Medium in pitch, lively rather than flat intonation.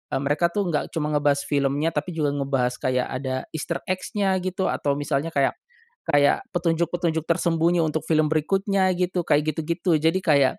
No: medium, 160 Hz; average, 3.3 semitones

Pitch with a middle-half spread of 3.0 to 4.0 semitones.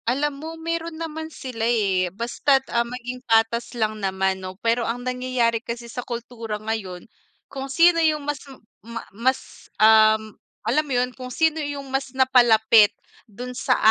Yes: average, 3.7 semitones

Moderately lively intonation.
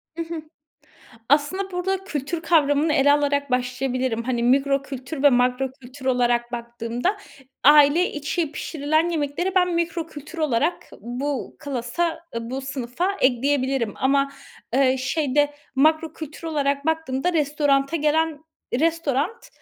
Yes: average, 3.7 semitones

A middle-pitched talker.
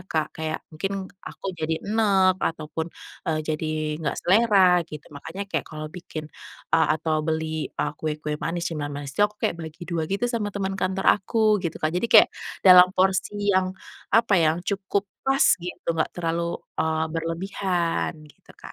Yes: medium, 170 Hz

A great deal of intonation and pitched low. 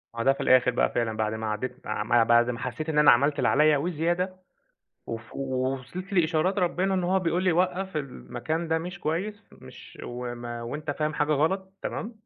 No: wide, 6.7 semitones; medium, 150 Hz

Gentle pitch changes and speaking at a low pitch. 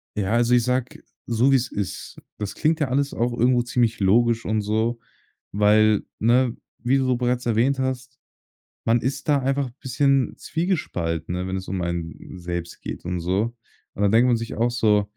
No: average, 3.8 semitones; low, 120 Hz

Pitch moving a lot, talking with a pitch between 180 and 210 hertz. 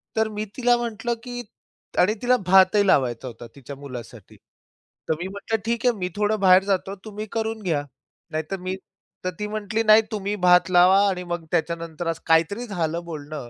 No: average, 4.8 semitones; medium, 185 Hz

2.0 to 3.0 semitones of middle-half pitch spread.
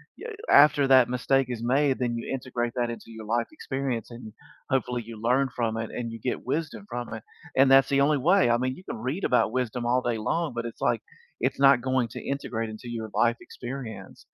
Yes: narrow, 2.6 semitones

